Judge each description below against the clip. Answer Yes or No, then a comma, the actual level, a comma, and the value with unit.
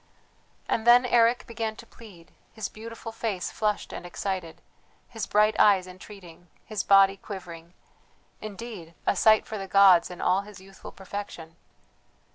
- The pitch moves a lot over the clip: No, average, 3.1 semitones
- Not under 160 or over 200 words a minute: No, average, 145 wpm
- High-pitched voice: Yes, high, 200 Hz